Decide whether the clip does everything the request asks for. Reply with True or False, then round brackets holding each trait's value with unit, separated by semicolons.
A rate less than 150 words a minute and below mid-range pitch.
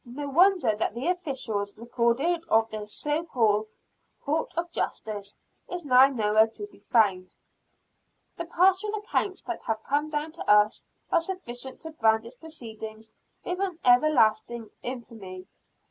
False (140 wpm; 245 Hz)